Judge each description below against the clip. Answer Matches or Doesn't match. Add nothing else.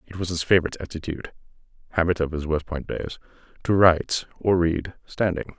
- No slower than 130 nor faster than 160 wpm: Matches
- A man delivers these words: Matches